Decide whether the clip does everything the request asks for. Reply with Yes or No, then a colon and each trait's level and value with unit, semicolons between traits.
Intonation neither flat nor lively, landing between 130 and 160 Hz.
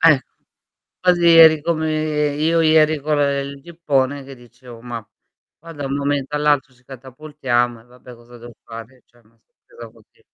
Yes: average, 4.0 semitones; medium, 140 Hz